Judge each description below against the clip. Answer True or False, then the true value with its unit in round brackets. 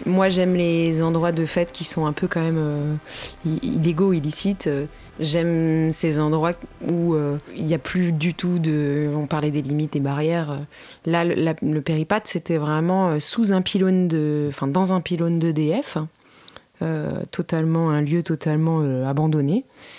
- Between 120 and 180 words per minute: True (170 wpm)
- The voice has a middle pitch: True (165 Hz)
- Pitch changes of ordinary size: False (2.3 semitones)